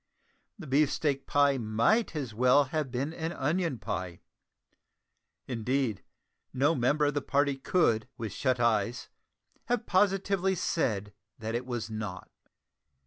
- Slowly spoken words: Yes, slow, 130 wpm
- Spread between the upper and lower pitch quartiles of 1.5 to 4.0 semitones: No, average, 5.2 semitones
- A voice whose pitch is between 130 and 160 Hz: Yes, low, 135 Hz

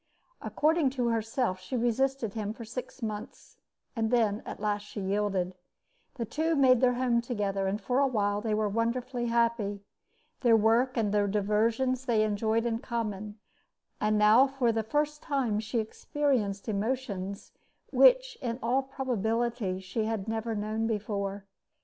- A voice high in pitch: Yes, high, 225 Hz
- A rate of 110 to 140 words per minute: No, average, 150 wpm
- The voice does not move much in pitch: No, average, 3.3 semitones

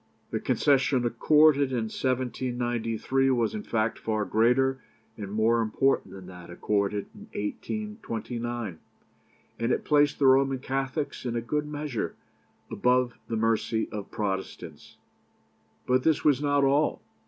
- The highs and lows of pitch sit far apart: No, average, 3.5 semitones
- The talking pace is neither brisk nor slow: No, slow, 130 wpm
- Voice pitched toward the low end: Yes, low, 125 Hz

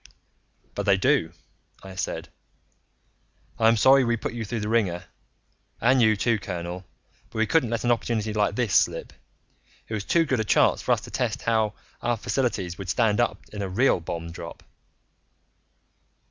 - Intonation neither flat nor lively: Yes, average, 3.6 semitones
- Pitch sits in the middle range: No, low, 110 Hz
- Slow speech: No, average, 175 wpm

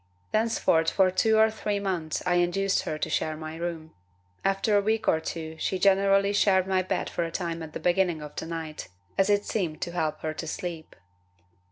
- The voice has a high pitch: No, medium, 175 Hz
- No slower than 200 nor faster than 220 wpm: Yes, fast, 205 wpm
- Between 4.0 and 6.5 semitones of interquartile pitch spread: No, average, 3.6 semitones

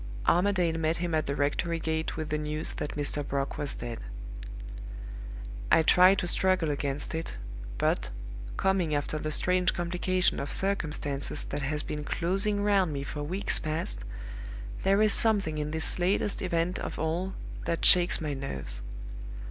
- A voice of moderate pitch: Yes, medium, 160 Hz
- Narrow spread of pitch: No, average, 3.8 semitones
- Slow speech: No, average, 155 wpm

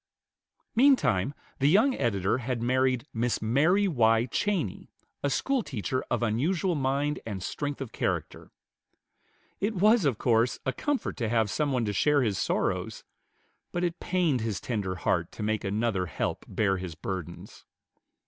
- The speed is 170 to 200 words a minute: No, average, 150 wpm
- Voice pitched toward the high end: No, low, 125 Hz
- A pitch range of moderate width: No, wide, 6.3 semitones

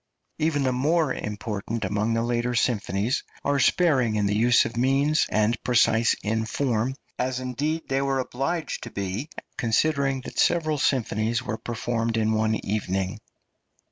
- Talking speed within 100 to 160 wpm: Yes, average, 150 wpm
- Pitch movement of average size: Yes, average, 3.8 semitones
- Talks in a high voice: No, low, 120 Hz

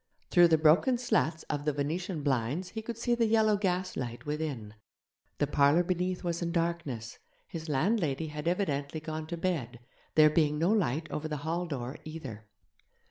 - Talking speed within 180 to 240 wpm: No, average, 170 wpm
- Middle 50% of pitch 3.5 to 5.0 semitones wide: Yes, average, 3.8 semitones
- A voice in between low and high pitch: Yes, medium, 160 Hz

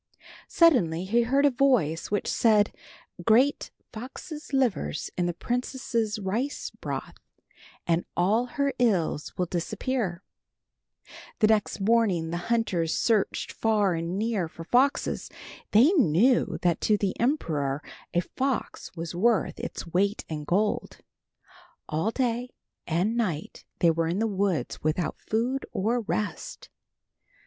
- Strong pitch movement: Yes, wide, 5.8 semitones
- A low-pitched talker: No, high, 210 Hz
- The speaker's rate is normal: No, slow, 130 wpm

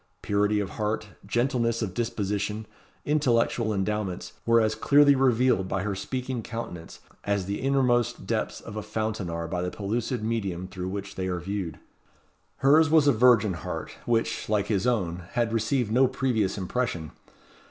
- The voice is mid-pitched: No, low, 110 Hz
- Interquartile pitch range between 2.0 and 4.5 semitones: Yes, average, 3.8 semitones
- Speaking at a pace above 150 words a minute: Yes, average, 160 wpm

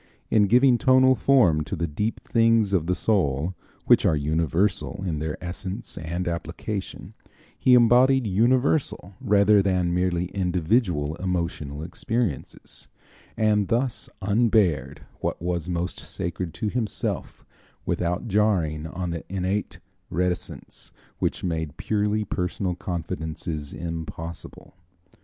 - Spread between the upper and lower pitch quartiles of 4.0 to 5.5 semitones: Yes, average, 4.3 semitones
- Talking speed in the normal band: No, slow, 115 wpm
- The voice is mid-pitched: No, very low, 90 Hz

